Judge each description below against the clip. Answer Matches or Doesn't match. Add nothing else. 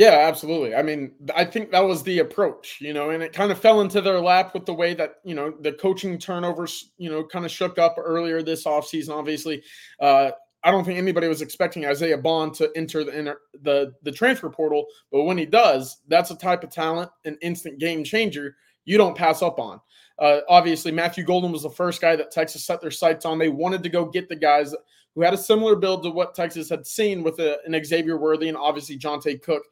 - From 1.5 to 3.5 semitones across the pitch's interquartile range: Matches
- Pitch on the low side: Doesn't match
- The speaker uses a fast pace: Matches